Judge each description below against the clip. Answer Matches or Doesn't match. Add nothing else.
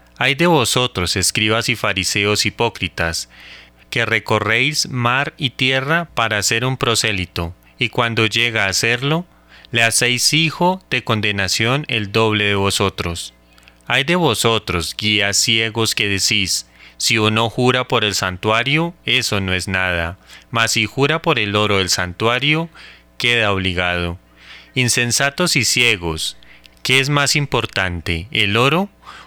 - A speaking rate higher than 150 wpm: Doesn't match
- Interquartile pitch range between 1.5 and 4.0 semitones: Doesn't match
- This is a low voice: Matches